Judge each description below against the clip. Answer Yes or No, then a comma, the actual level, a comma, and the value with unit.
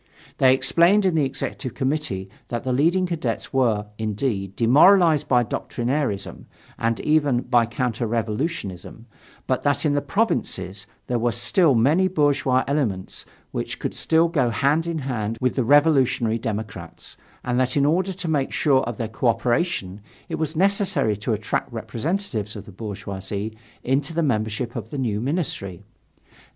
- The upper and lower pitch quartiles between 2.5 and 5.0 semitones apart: No, wide, 5.5 semitones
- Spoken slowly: No, average, 155 wpm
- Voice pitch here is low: Yes, low, 125 Hz